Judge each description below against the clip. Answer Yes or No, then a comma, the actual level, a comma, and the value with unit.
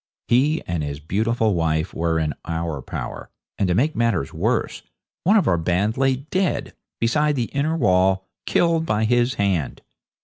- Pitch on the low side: Yes, low, 105 Hz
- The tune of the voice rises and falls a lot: Yes, wide, 8.0 semitones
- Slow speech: No, average, 165 wpm